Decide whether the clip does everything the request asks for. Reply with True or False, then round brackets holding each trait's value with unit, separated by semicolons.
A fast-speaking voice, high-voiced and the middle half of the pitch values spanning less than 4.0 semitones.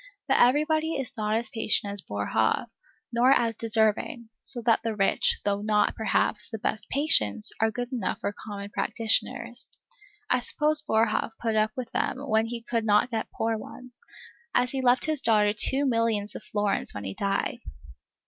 False (175 wpm; 225 Hz; 2.9 semitones)